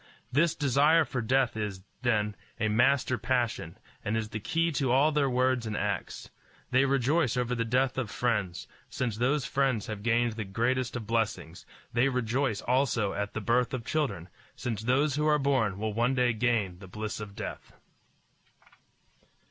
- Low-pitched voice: Yes, low, 120 Hz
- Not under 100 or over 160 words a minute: No, average, 170 wpm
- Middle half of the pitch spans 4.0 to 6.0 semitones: No, average, 3.6 semitones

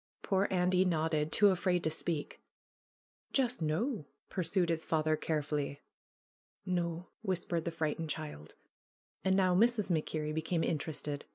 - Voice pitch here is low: No, medium, 165 Hz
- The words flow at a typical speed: No, slow, 125 wpm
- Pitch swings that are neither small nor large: Yes, average, 3.1 semitones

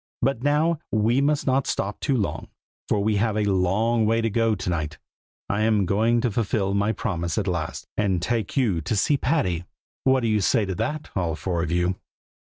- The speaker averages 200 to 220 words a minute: Yes, fast, 205 wpm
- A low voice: Yes, low, 105 Hz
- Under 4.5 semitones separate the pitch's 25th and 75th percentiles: Yes, average, 4.1 semitones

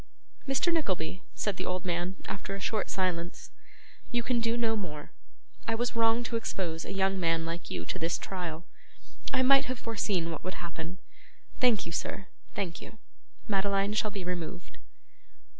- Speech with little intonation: No, average, 4.7 semitones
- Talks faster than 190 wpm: No, average, 170 wpm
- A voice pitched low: No, high, 195 Hz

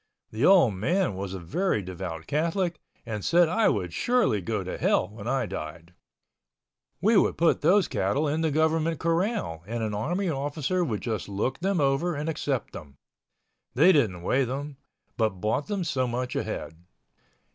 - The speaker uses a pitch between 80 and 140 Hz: Yes, low, 135 Hz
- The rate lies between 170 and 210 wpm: Yes, average, 175 wpm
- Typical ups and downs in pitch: No, wide, 8.5 semitones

